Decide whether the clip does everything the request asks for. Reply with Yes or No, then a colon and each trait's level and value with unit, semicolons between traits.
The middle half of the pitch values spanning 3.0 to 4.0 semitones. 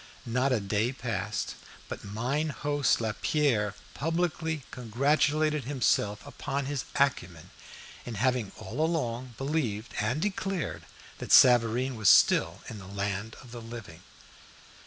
No: average, 4.9 semitones